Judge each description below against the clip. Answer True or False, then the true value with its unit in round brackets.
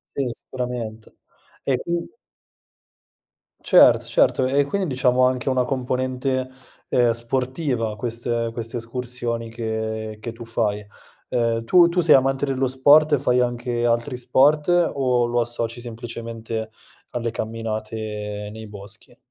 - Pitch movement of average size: False (2.2 semitones)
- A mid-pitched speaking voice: False (120 Hz)